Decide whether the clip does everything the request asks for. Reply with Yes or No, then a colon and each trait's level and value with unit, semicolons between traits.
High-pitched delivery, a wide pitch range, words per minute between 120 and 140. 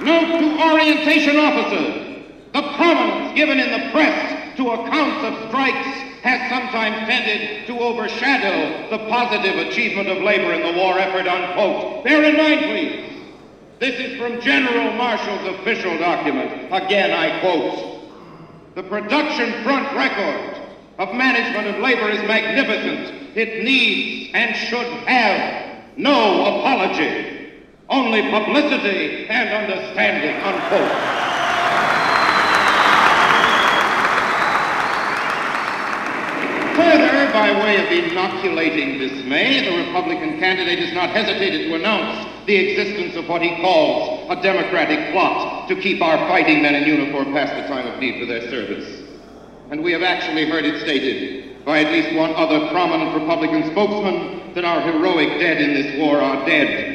Yes: very high, 250 Hz; wide, 7.0 semitones; slow, 135 wpm